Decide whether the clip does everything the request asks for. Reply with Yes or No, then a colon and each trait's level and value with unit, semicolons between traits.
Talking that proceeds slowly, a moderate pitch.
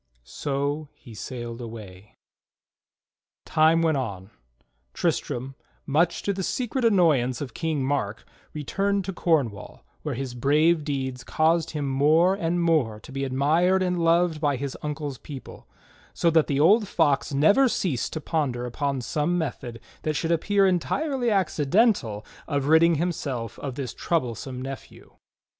No: average, 145 wpm; medium, 150 Hz